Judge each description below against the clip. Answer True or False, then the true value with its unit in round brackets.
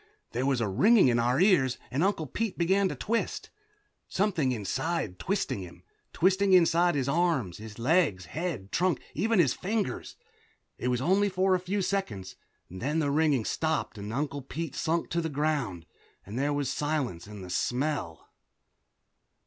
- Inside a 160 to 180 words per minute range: True (170 wpm)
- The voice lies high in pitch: False (150 Hz)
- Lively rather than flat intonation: True (7.0 semitones)